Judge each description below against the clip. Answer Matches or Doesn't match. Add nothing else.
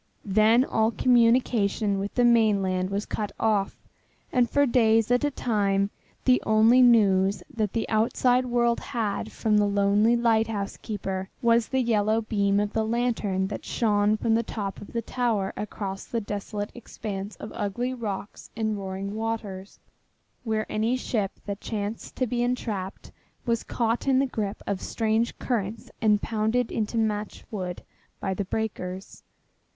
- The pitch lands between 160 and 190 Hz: Doesn't match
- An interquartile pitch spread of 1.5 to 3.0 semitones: Matches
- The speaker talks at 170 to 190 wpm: Doesn't match